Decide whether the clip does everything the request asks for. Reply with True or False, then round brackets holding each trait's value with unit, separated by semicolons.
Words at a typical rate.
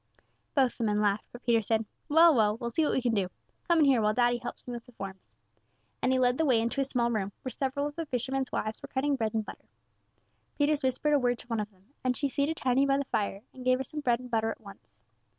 False (270 wpm)